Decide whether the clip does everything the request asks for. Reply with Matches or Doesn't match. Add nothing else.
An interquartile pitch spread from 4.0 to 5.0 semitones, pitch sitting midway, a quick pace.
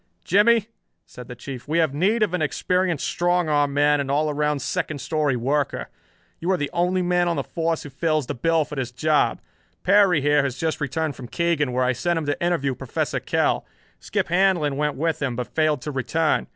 Doesn't match